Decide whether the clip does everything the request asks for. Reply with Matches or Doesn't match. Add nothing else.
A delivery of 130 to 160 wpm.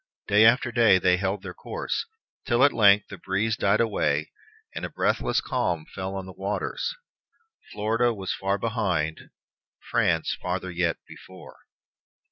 Matches